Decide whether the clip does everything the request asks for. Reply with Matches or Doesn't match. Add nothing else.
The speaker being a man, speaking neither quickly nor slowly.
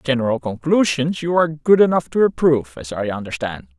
Matches